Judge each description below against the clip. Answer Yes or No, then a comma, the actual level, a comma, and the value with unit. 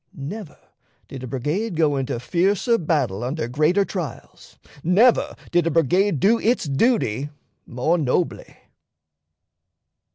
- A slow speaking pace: Yes, slow, 120 wpm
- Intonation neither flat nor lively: No, wide, 6.4 semitones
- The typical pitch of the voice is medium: Yes, medium, 160 Hz